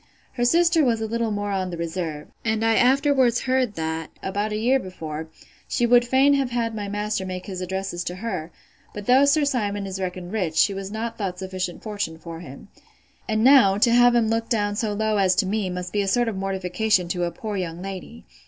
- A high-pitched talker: Yes, high, 205 Hz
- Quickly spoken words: Yes, fast, 220 wpm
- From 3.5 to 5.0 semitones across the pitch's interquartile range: Yes, average, 4.1 semitones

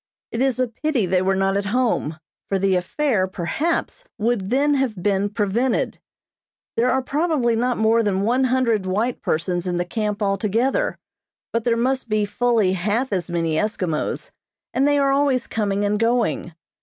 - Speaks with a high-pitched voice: Yes, high, 220 Hz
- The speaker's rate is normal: Yes, average, 170 wpm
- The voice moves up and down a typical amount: Yes, average, 4.7 semitones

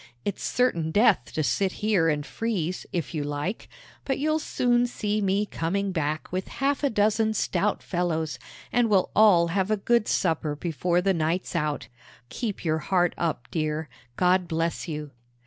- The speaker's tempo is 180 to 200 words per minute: No, average, 165 wpm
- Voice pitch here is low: No, medium, 180 Hz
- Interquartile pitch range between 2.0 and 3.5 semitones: No, average, 4.8 semitones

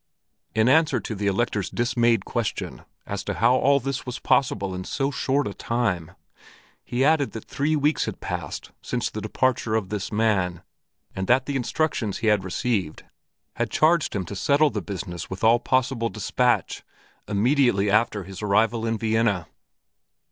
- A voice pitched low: Yes, low, 115 Hz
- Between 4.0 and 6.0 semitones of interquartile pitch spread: Yes, average, 4.4 semitones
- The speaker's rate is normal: Yes, average, 165 wpm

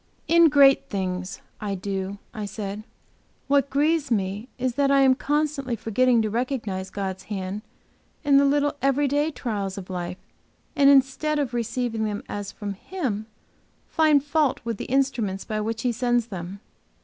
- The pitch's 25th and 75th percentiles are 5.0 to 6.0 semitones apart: Yes, wide, 5.6 semitones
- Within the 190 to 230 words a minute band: No, average, 160 wpm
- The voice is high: Yes, high, 240 Hz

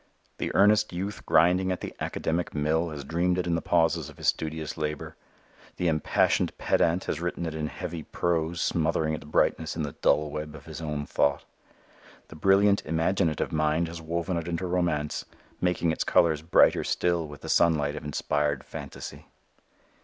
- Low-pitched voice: Yes, very low, 80 Hz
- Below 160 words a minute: No, average, 175 wpm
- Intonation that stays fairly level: Yes, narrow, 2.2 semitones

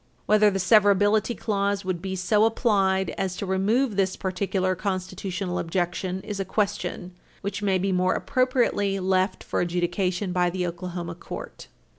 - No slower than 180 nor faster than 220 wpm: No, average, 150 wpm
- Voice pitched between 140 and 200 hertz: Yes, high, 190 Hz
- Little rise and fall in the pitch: Yes, narrow, 1.9 semitones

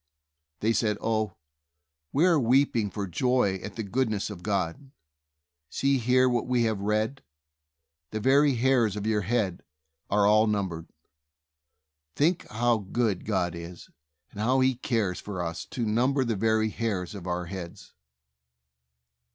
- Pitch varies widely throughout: No, average, 4.1 semitones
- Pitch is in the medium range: No, low, 110 Hz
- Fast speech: No, average, 145 wpm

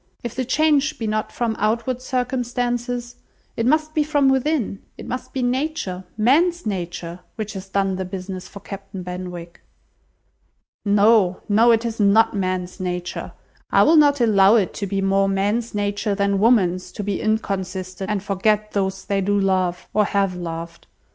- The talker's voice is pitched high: Yes, high, 205 Hz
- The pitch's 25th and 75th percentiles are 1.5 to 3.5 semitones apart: No, average, 4.1 semitones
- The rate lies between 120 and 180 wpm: Yes, average, 165 wpm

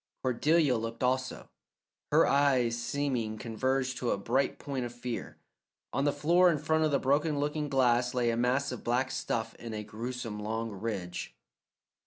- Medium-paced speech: Yes, average, 170 wpm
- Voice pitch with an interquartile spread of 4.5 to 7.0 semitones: No, average, 3.5 semitones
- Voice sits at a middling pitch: No, low, 125 Hz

